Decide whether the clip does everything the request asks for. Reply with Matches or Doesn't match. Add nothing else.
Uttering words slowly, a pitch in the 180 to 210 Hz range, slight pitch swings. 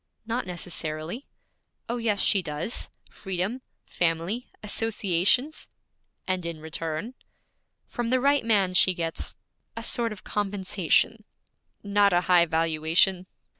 Doesn't match